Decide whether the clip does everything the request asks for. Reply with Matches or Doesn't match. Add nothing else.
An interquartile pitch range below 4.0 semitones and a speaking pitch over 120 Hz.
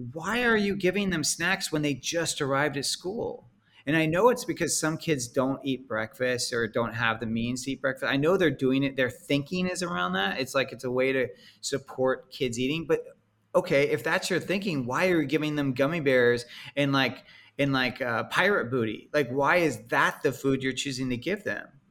Doesn't match